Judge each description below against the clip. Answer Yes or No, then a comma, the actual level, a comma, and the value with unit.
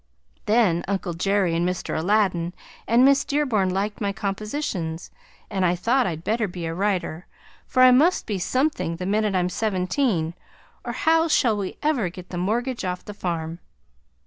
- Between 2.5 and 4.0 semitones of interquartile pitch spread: No, average, 4.8 semitones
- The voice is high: Yes, high, 195 Hz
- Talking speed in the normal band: Yes, average, 170 wpm